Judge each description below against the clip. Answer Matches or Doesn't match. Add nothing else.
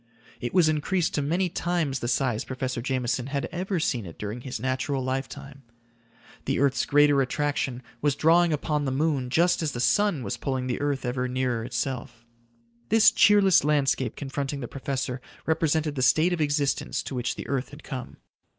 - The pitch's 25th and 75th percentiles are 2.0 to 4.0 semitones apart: Matches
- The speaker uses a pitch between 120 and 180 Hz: Matches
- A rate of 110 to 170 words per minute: Doesn't match